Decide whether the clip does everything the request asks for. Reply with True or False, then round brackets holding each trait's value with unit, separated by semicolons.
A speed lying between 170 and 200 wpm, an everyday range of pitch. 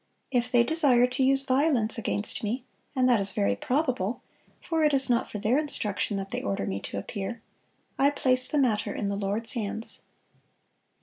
True (185 wpm; 4.7 semitones)